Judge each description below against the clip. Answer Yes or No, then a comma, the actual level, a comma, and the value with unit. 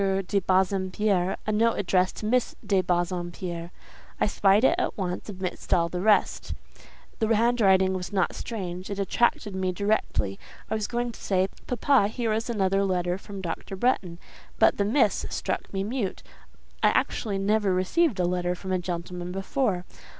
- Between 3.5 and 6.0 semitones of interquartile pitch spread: No, average, 2.8 semitones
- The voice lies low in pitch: No, high, 195 Hz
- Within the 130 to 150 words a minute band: No, average, 165 wpm